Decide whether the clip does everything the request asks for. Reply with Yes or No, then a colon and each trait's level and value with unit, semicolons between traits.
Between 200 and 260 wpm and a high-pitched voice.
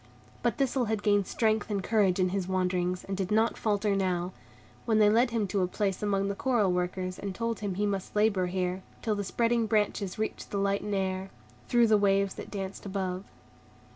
Yes: fast, 205 wpm; high, 200 Hz